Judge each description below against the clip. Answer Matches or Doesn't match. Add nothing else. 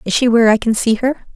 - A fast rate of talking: Matches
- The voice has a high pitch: Matches